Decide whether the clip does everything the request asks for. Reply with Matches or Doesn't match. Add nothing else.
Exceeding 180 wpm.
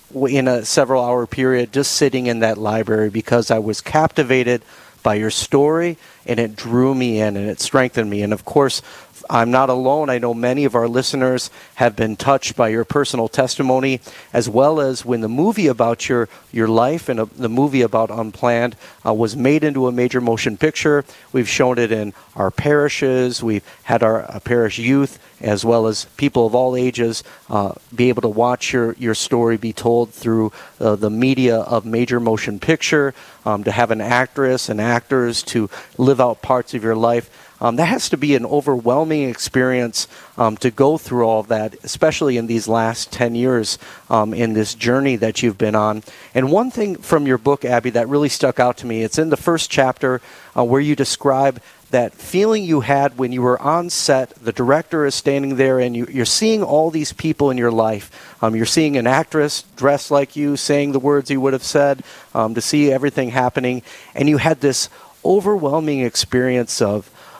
Matches